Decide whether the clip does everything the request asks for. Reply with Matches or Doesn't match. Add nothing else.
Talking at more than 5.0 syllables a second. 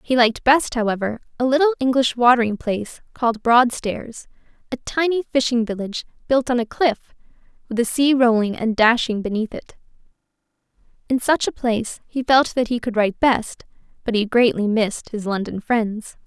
Matches